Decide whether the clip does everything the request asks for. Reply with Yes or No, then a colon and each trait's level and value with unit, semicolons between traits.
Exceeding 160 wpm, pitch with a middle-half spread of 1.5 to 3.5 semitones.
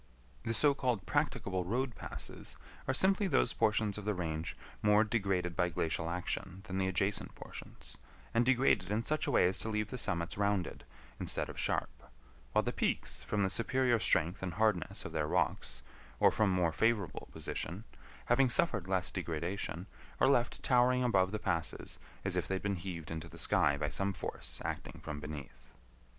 No: average, 180 wpm; average, 4.7 semitones